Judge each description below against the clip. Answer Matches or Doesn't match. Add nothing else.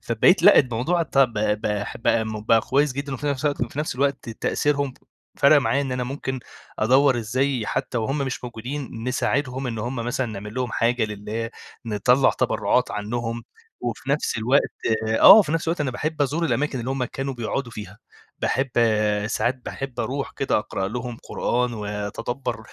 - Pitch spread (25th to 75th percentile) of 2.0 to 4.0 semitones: Matches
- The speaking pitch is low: Matches